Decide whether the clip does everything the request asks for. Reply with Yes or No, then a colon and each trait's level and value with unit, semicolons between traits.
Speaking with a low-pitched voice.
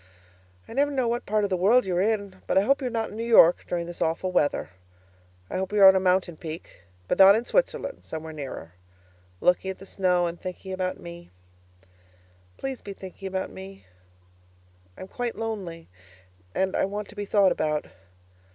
No: high, 190 Hz